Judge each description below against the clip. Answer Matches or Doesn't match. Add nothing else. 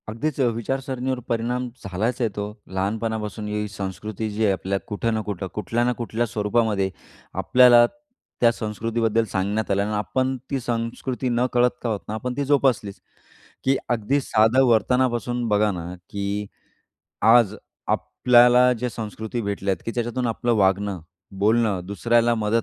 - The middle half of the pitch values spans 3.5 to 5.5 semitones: Doesn't match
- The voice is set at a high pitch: Doesn't match